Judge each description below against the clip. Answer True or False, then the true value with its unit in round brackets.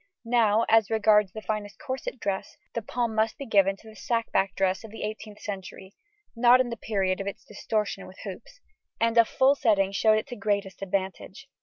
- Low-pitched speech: False (215 Hz)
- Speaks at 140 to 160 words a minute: False (200 wpm)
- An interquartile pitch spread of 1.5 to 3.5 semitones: True (2.7 semitones)